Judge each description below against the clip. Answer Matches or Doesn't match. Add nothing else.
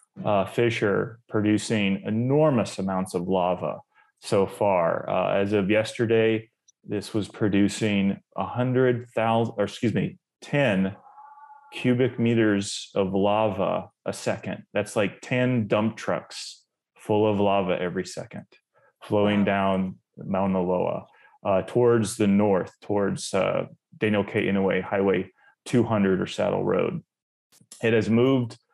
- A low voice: Matches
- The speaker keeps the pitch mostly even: Doesn't match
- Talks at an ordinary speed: Doesn't match